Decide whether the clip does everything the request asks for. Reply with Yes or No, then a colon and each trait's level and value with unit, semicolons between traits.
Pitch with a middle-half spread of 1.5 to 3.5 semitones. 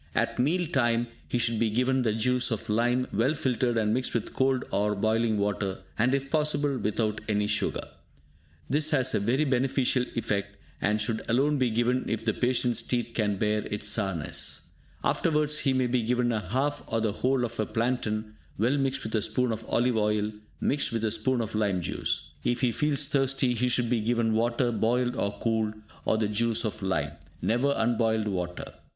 Yes: average, 3.0 semitones